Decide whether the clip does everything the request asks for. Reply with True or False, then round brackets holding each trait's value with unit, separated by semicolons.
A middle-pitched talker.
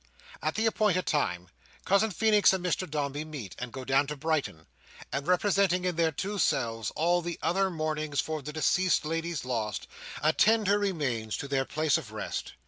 True (155 Hz)